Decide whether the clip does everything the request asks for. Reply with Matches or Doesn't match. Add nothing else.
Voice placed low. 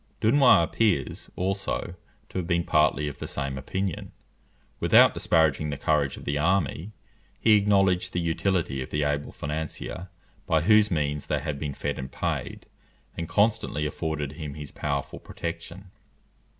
Matches